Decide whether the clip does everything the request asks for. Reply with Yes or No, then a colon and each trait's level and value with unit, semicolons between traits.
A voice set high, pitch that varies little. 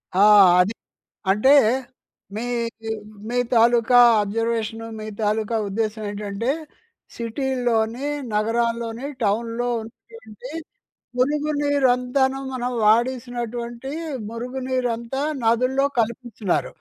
Yes: high, 235 Hz; narrow, 2.1 semitones